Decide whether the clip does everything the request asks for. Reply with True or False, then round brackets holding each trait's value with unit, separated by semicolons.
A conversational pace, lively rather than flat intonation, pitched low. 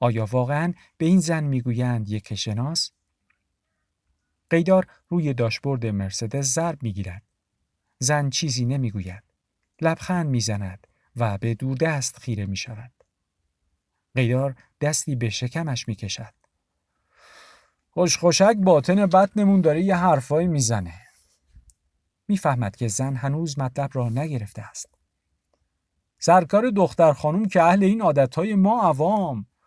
True (115 wpm; 7.8 semitones; 130 Hz)